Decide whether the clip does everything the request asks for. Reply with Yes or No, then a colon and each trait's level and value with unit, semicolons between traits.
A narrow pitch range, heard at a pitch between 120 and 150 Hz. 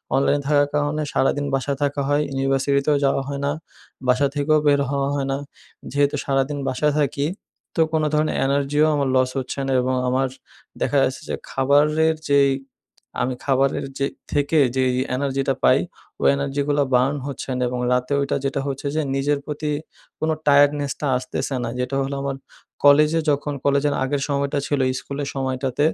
Yes: narrow, 1.2 semitones; medium, 140 Hz